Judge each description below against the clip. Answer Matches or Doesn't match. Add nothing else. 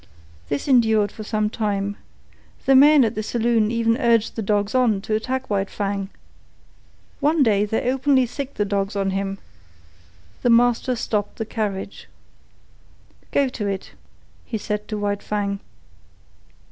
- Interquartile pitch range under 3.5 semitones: Matches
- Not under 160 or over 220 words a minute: Doesn't match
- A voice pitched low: Doesn't match